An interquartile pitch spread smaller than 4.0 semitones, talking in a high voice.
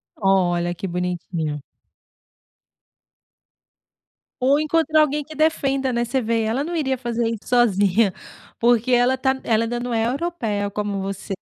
No: average, 5.1 semitones; high, 235 Hz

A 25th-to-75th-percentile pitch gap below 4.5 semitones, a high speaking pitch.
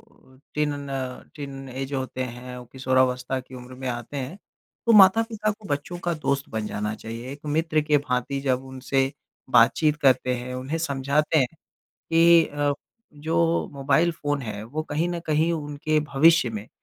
No: average, 3.4 semitones; medium, 140 Hz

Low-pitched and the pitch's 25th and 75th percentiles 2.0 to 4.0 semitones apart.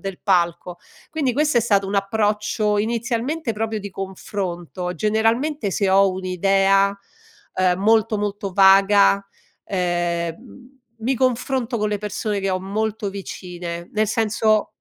No: high, 205 Hz; average, 2.7 semitones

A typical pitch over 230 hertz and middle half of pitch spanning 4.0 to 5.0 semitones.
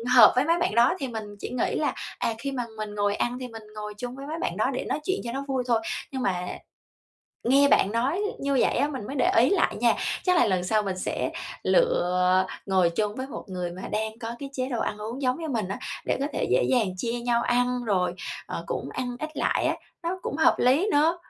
Yes: high, 245 Hz; average, 4.7 semitones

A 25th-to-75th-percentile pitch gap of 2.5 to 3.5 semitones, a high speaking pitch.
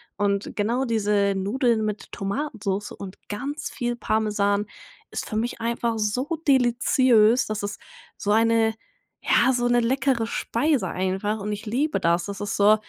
Yes: average, 2.9 semitones; high, 220 Hz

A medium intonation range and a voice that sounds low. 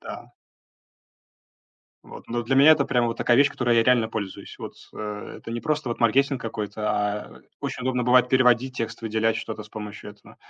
Yes: average, 3.1 semitones; low, 120 Hz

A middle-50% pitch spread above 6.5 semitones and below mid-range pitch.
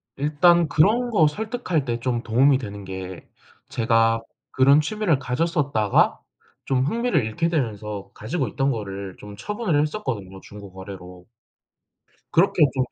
Yes: wide, 7.9 semitones; low, 130 Hz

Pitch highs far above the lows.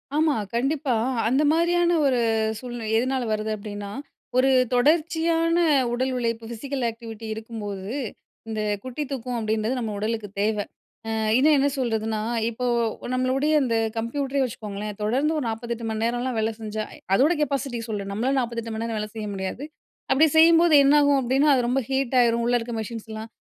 No: average, 3.8 semitones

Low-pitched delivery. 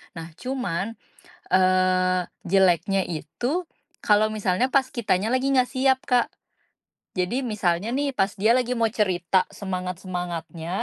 No: high, 190 Hz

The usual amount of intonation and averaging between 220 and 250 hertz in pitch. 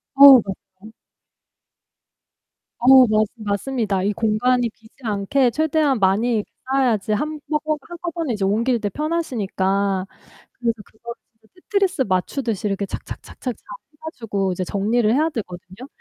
Yes: average, 5.0 semitones; high, 225 Hz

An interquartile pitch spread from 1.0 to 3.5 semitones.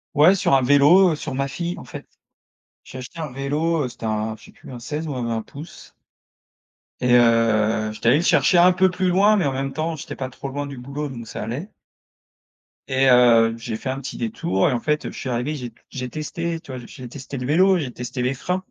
No: average, 4.7 semitones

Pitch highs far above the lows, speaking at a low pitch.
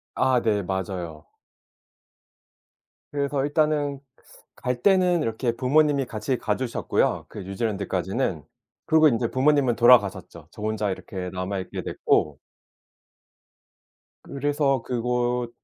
Yes: wide, 5.8 semitones; low, 120 Hz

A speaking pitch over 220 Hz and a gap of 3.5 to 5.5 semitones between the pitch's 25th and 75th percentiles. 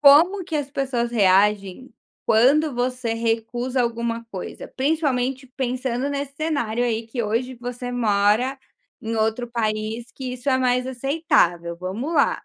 No: high, 245 Hz; average, 3.1 semitones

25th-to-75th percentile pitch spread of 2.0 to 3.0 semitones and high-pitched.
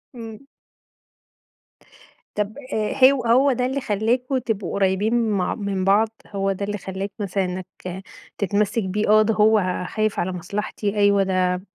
Yes: narrow, 2.6 semitones; high, 205 Hz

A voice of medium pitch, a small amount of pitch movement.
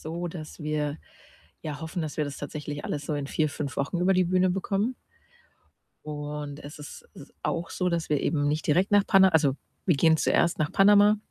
No: medium, 155 Hz; average, 3.6 semitones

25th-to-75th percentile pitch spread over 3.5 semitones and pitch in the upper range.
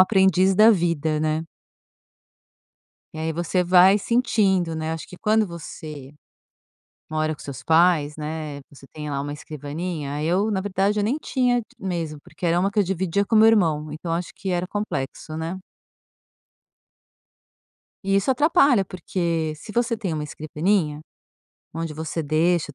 No: average, 4.0 semitones; medium, 170 Hz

